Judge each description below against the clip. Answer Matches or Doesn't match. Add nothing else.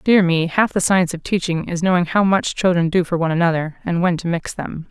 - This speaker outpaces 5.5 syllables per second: Matches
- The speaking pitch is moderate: Matches